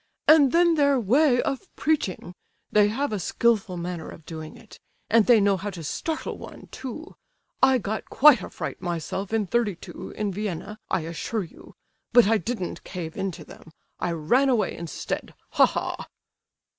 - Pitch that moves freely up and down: Yes, wide, 6.0 semitones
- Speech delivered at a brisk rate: No, average, 170 wpm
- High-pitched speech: Yes, high, 210 Hz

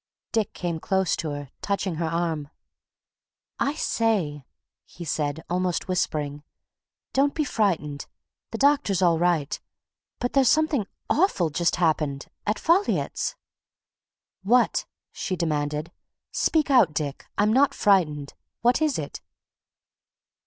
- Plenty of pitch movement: Yes, wide, 7.5 semitones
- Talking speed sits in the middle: No, slow, 120 wpm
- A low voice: No, medium, 180 Hz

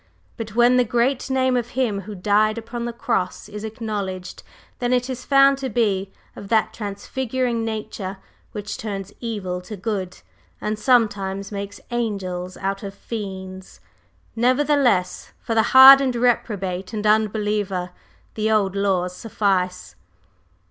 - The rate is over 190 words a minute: No, slow, 135 wpm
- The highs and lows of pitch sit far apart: No, average, 3.5 semitones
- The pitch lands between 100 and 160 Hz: No, high, 215 Hz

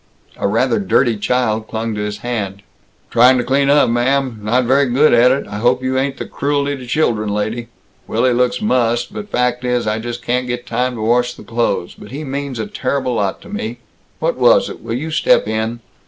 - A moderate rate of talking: No, fast, 215 wpm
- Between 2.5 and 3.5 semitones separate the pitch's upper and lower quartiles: Yes, average, 2.8 semitones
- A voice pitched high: No, low, 125 Hz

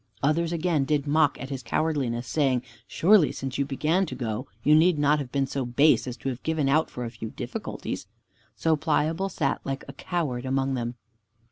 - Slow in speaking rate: No, average, 200 wpm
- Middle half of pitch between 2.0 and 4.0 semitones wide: Yes, average, 3.3 semitones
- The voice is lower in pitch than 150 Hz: Yes, medium, 140 Hz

